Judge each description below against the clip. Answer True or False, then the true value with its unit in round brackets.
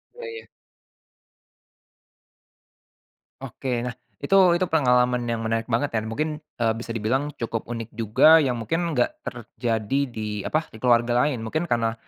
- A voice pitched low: True (120 Hz)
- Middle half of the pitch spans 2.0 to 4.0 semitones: False (4.5 semitones)